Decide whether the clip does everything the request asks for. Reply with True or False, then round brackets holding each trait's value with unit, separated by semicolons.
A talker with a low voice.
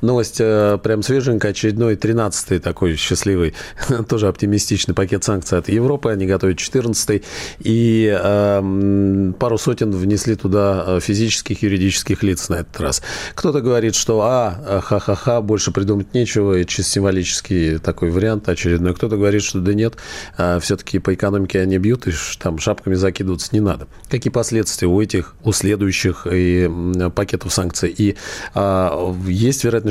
True (100 Hz)